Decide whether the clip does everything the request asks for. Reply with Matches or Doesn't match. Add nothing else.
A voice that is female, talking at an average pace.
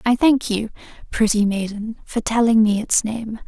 Matches